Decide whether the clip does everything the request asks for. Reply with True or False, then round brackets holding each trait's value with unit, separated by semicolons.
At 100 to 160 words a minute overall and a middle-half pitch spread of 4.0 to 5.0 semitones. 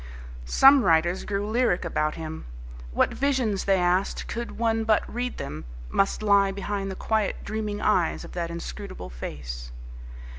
True (150 wpm; 4.4 semitones)